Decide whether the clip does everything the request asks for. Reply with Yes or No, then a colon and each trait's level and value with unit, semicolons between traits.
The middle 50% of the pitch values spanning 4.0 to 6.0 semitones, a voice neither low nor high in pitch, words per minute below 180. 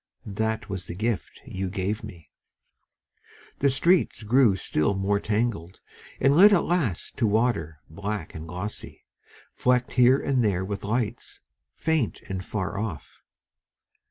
No: average, 4.6 semitones; low, 105 Hz; slow, 135 wpm